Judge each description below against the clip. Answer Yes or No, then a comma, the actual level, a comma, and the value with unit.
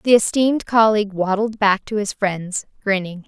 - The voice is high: Yes, high, 205 Hz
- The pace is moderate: Yes, average, 165 wpm